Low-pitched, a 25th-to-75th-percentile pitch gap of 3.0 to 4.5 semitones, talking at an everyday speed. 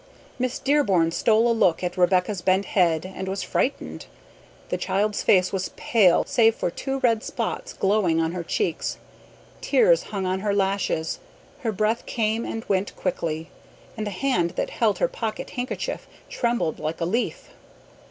No: high, 200 Hz; average, 4.0 semitones; average, 160 wpm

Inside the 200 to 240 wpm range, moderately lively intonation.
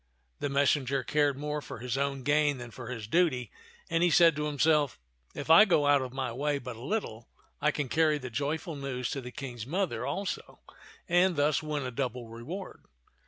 Yes: fast, 205 wpm; average, 3.3 semitones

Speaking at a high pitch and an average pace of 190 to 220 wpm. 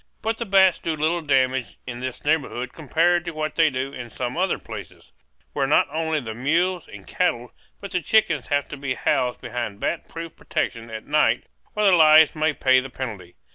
No: medium, 150 Hz; average, 200 wpm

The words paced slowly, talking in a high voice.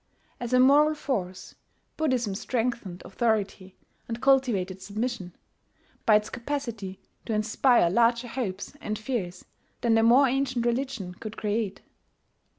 Yes: slow, 125 wpm; high, 230 Hz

